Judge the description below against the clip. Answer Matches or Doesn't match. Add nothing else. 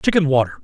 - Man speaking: Matches